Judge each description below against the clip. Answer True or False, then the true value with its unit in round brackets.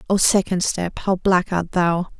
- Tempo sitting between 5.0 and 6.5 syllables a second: False (4.1 syllables/s)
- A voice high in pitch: False (180 Hz)